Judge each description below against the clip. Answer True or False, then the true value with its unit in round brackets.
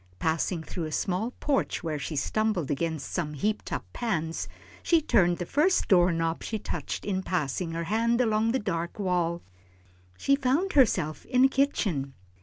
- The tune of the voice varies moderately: False (6.0 semitones)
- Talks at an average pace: True (170 wpm)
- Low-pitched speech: False (185 Hz)